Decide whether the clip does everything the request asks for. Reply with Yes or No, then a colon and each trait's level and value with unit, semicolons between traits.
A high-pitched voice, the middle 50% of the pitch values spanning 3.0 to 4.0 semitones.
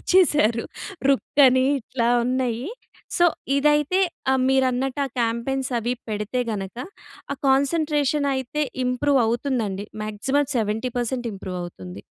Yes: very high, 255 Hz; average, 3.7 semitones